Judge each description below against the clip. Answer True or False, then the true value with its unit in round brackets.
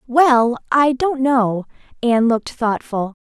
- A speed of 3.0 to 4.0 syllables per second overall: True (3.9 syllables/s)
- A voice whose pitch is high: True (245 Hz)